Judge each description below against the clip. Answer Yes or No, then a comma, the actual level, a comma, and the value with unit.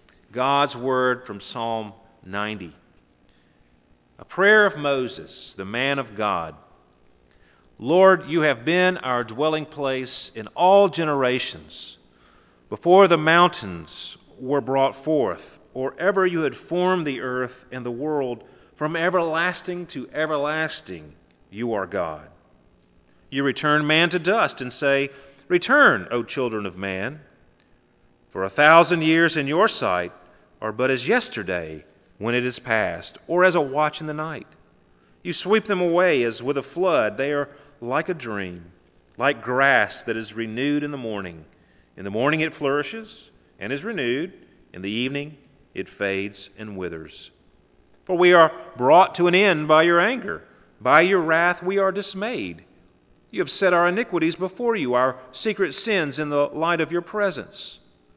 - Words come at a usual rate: Yes, average, 155 wpm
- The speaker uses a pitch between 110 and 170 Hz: Yes, low, 135 Hz